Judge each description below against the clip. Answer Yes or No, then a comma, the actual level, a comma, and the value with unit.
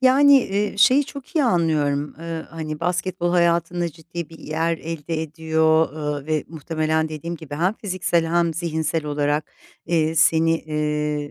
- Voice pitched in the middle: Yes, medium, 160 Hz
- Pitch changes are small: Yes, narrow, 1.9 semitones